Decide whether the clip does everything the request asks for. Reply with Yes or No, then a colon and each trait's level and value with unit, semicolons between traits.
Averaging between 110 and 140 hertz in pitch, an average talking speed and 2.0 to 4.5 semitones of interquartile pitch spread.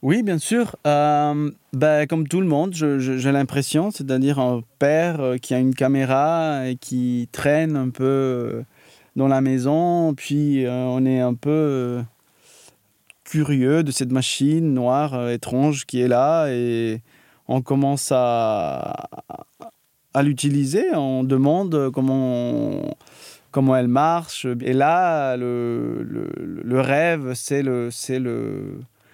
No: low, 135 Hz; slow, 135 wpm; average, 2.7 semitones